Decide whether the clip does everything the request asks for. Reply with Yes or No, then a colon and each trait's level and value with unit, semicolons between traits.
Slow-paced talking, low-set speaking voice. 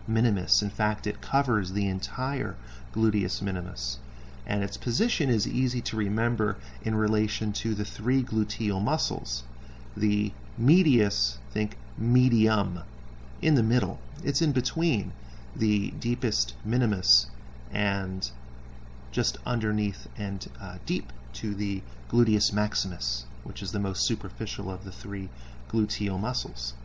Yes: slow, 125 wpm; low, 105 Hz